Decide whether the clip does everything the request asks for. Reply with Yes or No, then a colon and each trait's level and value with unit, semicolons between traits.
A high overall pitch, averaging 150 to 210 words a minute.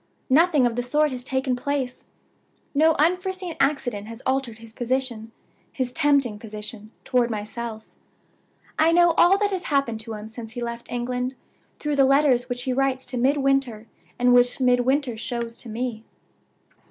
Yes: very high, 250 Hz; average, 160 wpm